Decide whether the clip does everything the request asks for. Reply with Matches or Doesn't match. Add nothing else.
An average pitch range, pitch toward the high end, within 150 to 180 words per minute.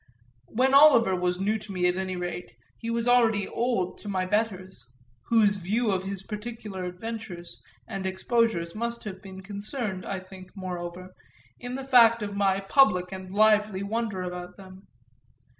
Matches